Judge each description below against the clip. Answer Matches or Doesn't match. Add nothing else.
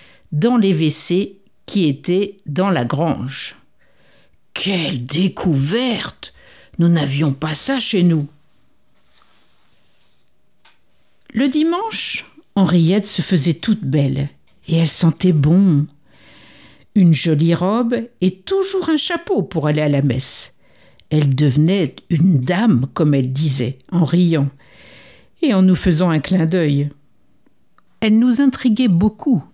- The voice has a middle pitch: Matches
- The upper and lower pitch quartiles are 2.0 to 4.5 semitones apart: Doesn't match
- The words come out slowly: Matches